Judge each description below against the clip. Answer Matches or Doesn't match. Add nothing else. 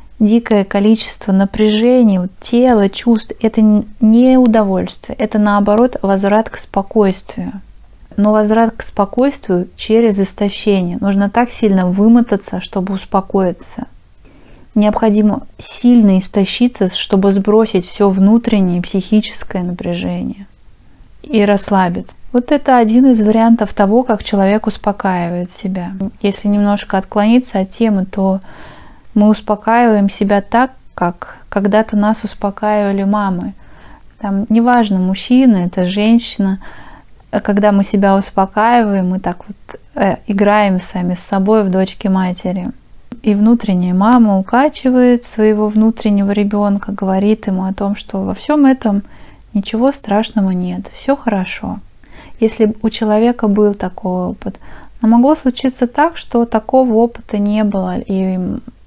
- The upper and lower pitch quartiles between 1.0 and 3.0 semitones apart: Matches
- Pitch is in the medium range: Doesn't match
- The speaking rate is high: Doesn't match